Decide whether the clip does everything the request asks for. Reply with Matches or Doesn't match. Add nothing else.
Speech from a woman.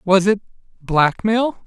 Doesn't match